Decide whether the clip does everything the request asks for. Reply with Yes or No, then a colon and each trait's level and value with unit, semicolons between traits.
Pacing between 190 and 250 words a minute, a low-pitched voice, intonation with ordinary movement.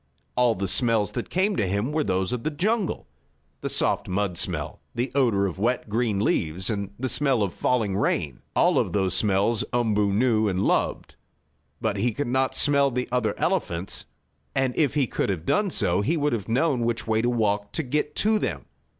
Yes: average, 200 wpm; low, 115 Hz; average, 4.8 semitones